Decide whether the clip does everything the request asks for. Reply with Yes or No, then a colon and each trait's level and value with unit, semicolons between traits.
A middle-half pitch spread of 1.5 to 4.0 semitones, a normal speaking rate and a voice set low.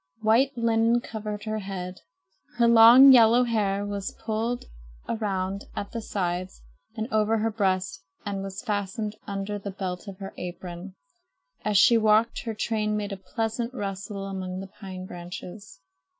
No: narrow, 2.6 semitones; average, 150 wpm; high, 205 Hz